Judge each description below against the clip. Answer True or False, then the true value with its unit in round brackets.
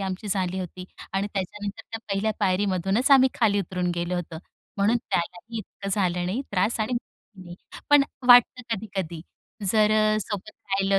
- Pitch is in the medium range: False (195 Hz)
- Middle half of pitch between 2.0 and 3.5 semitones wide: True (2.9 semitones)